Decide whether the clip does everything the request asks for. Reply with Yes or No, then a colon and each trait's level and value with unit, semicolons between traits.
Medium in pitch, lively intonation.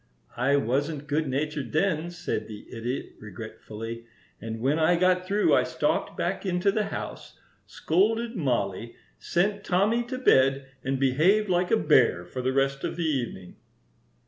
Yes: medium, 145 Hz; wide, 6.5 semitones